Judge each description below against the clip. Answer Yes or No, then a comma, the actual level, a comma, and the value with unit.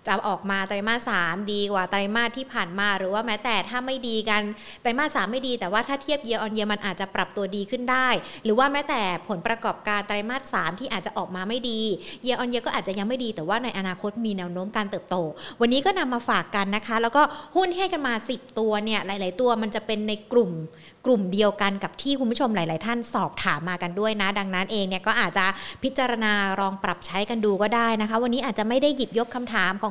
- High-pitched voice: Yes, high, 215 Hz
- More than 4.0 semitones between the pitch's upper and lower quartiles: No, average, 3.7 semitones